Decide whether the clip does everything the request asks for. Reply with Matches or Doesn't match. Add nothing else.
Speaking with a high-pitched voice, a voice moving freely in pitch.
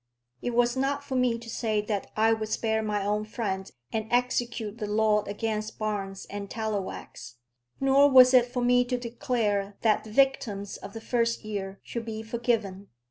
Doesn't match